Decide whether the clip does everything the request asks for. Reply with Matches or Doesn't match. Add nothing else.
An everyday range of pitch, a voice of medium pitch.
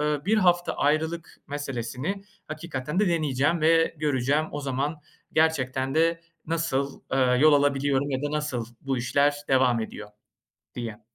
Matches